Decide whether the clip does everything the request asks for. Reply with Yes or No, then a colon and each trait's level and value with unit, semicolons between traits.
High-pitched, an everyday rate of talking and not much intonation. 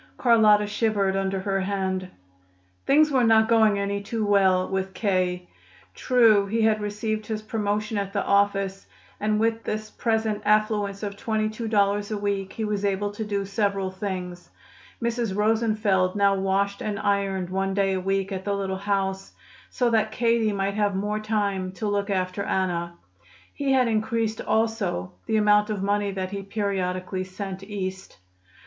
Yes: high, 205 Hz; average, 165 wpm; narrow, 1.9 semitones